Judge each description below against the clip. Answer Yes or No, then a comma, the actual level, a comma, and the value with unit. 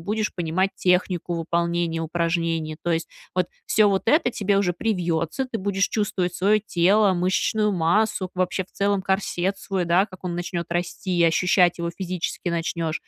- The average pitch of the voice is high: No, medium, 180 Hz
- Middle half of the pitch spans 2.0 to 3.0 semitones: Yes, narrow, 2.5 semitones